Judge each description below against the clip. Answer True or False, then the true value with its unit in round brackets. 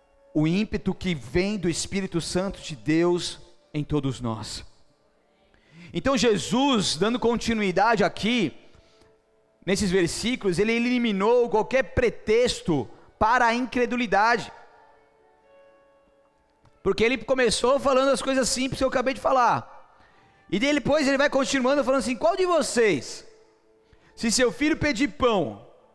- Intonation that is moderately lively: False (6.9 semitones)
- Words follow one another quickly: False (125 wpm)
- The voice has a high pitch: True (230 Hz)